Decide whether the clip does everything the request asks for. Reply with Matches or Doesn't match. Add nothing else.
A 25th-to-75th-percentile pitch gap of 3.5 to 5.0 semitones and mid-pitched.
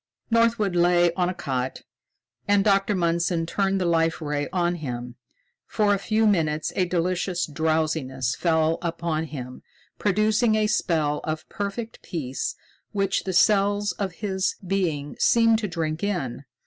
Matches